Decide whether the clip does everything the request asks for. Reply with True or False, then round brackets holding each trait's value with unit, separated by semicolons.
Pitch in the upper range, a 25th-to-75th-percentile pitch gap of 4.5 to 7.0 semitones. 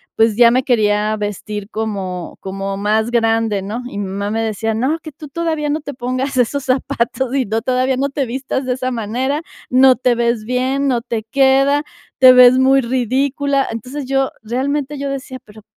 False (250 Hz; 3.5 semitones)